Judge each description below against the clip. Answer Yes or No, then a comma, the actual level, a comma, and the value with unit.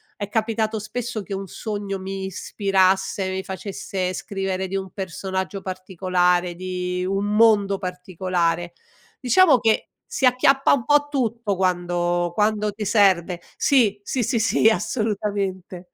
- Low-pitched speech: No, high, 195 Hz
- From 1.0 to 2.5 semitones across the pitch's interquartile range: No, average, 2.9 semitones